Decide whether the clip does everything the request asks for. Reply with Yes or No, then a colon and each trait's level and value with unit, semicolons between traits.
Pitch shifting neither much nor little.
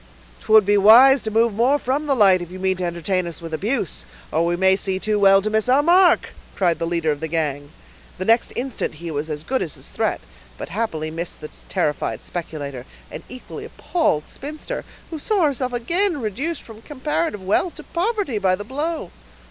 No: wide, 8.0 semitones